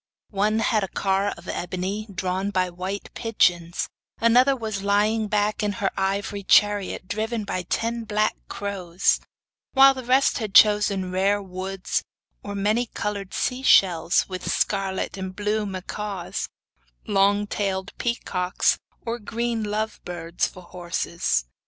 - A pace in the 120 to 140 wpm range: Yes, slow, 135 wpm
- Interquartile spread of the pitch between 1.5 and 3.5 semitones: Yes, narrow, 2.4 semitones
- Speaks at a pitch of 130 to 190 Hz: No, high, 200 Hz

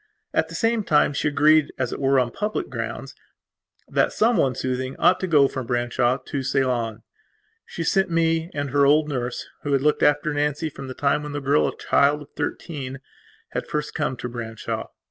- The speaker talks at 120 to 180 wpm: No, average, 195 wpm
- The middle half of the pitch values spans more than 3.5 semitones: No, average, 2.8 semitones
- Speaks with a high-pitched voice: No, medium, 145 Hz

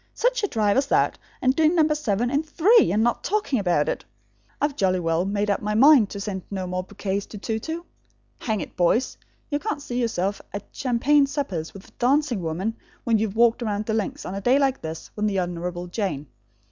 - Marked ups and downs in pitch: Yes, wide, 6.3 semitones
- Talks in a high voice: Yes, high, 220 Hz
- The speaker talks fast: Yes, fast, 215 wpm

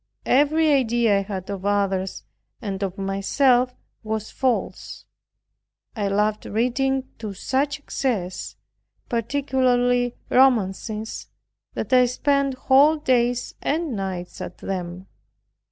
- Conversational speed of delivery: No, slow, 105 wpm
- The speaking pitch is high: Yes, high, 240 Hz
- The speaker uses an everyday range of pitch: Yes, average, 5.0 semitones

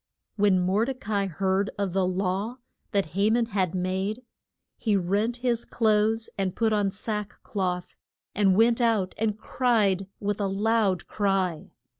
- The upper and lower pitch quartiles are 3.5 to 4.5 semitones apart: No, average, 2.7 semitones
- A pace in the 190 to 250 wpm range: No, average, 160 wpm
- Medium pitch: No, high, 205 Hz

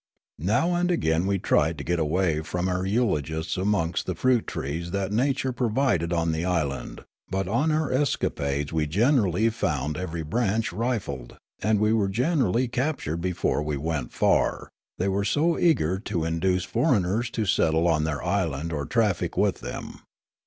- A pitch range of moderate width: No, wide, 6.2 semitones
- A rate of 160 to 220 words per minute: Yes, average, 170 wpm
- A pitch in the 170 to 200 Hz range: No, very low, 95 Hz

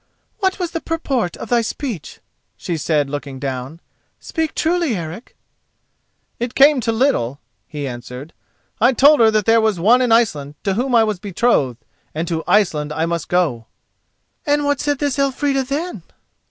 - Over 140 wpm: Yes, average, 165 wpm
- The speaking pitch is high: Yes, high, 220 Hz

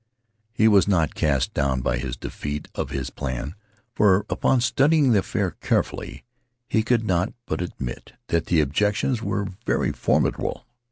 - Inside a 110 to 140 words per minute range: No, average, 155 wpm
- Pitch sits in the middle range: No, very low, 90 Hz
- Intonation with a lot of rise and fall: Yes, wide, 7.7 semitones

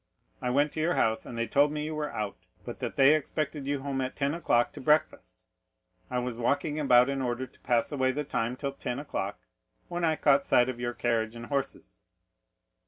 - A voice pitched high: No, low, 135 Hz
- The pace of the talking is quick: Yes, fast, 215 wpm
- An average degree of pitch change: Yes, average, 3.5 semitones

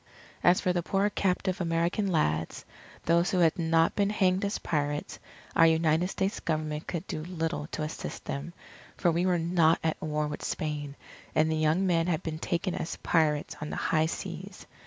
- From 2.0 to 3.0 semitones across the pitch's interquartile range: Yes, narrow, 2.6 semitones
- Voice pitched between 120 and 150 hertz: No, medium, 165 Hz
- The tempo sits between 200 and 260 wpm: No, average, 185 wpm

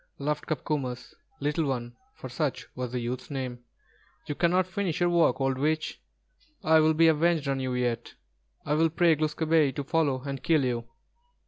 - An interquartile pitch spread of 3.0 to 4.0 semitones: Yes, average, 3.7 semitones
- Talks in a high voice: No, medium, 145 Hz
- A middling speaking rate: Yes, average, 180 wpm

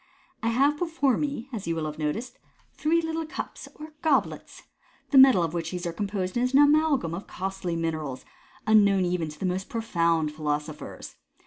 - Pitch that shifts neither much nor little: No, wide, 8.5 semitones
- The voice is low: No, high, 195 Hz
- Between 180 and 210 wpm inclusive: Yes, average, 185 wpm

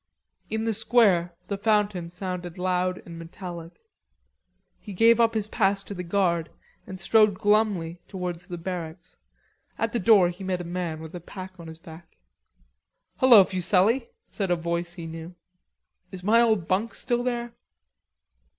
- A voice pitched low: No, medium, 185 Hz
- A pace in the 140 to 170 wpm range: Yes, average, 160 wpm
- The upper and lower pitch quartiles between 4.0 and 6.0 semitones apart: No, average, 3.5 semitones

